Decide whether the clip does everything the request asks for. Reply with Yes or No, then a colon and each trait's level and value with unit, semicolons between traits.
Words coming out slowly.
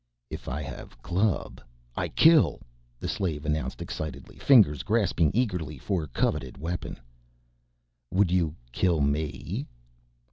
Yes: slow, 115 wpm